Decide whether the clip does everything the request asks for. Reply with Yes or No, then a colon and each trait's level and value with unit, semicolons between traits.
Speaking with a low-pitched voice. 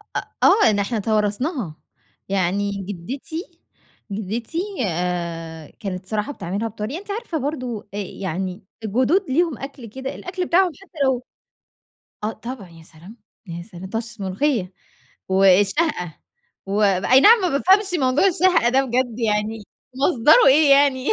No: high, 225 Hz